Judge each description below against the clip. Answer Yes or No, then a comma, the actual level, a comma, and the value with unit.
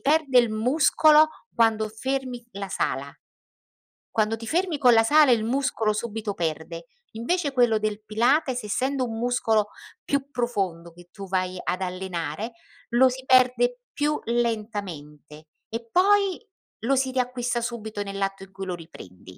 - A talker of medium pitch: No, high, 230 Hz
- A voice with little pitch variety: No, average, 4.7 semitones